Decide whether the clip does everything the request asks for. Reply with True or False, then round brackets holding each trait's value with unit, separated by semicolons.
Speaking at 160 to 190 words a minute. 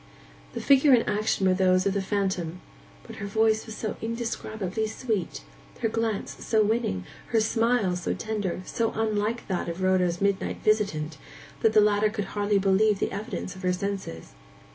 True (170 wpm)